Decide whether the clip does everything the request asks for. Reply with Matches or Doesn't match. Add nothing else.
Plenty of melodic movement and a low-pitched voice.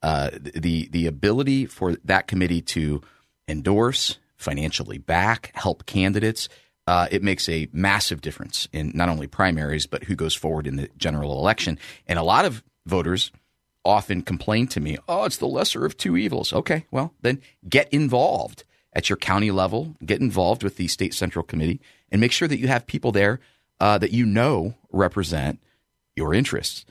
Matches